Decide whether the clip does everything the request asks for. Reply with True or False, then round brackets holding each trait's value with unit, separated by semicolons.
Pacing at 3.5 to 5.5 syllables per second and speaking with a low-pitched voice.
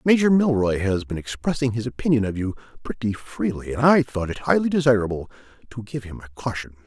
False (6.0 syllables/s; 120 Hz)